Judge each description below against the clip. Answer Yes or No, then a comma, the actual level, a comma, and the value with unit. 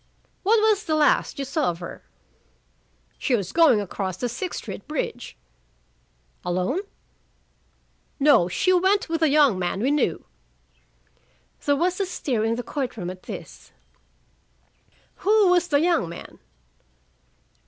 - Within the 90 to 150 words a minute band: Yes, average, 140 wpm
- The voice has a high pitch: Yes, very high, 285 Hz